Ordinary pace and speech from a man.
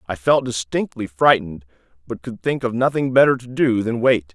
Yes: average, 195 wpm; male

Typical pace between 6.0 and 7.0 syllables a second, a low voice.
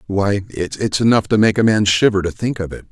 No: 5.4 syllables/s; low, 100 Hz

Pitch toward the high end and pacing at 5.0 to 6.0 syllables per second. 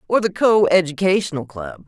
No: medium, 175 Hz; 5.3 syllables/s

